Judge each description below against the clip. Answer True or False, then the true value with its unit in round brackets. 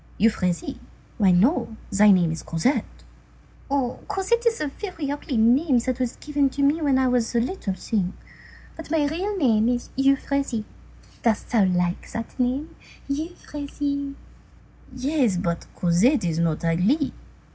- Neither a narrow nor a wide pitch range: False (5.9 semitones)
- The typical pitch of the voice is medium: False (255 Hz)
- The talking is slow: False (145 wpm)